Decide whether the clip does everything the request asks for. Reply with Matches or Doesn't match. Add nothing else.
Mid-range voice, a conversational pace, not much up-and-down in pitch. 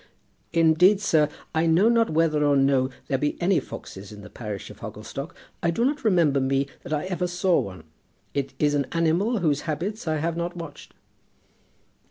Doesn't match